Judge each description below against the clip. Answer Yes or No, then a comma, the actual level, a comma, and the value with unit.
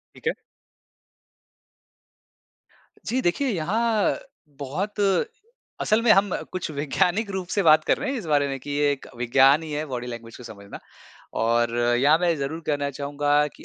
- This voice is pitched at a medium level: Yes, medium, 150 Hz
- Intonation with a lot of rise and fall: Yes, wide, 5.7 semitones